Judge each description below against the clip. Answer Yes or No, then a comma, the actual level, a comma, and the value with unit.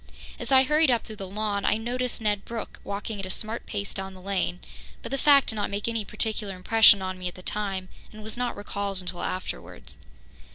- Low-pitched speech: No, high, 205 Hz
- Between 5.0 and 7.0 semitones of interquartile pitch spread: No, average, 2.8 semitones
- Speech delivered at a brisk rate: Yes, fast, 220 wpm